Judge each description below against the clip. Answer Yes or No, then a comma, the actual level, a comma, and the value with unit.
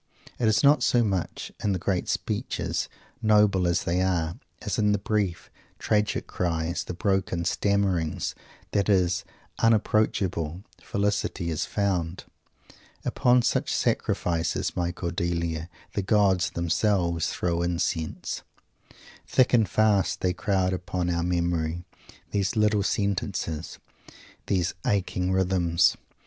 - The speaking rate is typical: No, slow, 120 wpm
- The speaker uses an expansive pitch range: No, average, 3.0 semitones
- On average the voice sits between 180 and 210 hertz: No, very low, 95 Hz